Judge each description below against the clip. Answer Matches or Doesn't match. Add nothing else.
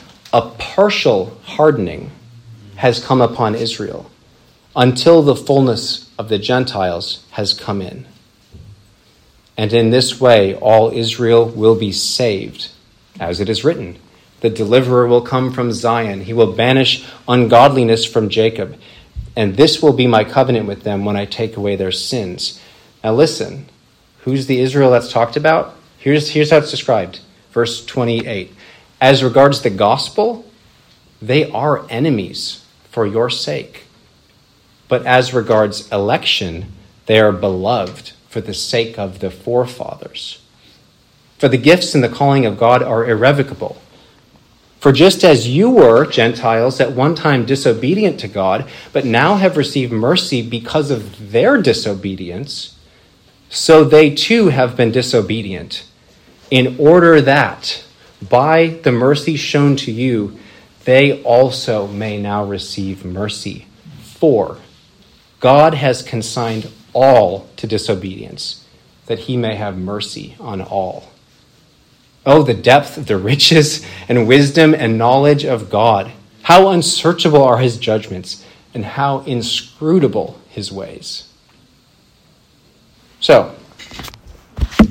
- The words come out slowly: Matches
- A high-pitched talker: Doesn't match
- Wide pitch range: Doesn't match